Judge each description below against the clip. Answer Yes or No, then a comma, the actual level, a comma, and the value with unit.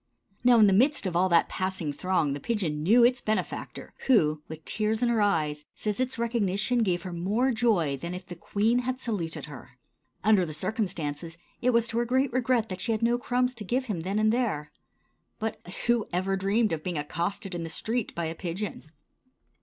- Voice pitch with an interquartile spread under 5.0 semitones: No, wide, 5.6 semitones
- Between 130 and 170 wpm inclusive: No, fast, 205 wpm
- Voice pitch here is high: Yes, high, 200 Hz